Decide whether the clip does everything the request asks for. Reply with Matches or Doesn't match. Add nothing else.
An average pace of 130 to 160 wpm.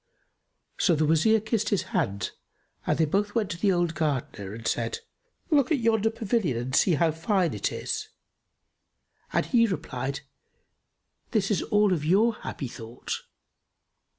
Matches